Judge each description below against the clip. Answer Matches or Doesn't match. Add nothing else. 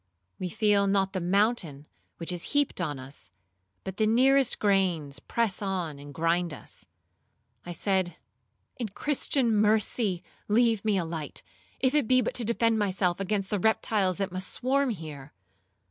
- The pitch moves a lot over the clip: Doesn't match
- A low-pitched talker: Doesn't match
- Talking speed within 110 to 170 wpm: Matches